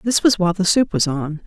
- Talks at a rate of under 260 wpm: No, fast, 285 wpm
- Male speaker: No, female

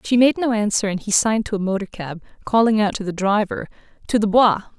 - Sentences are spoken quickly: Yes, fast, 240 wpm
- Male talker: No, female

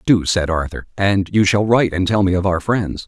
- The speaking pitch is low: Yes, very low, 95 Hz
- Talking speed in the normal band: No, fast, 255 wpm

